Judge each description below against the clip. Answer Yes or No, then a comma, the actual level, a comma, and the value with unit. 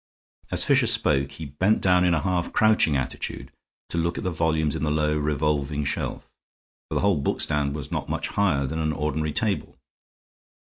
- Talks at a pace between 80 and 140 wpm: No, average, 185 wpm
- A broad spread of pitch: No, average, 2.9 semitones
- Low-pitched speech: Yes, very low, 75 Hz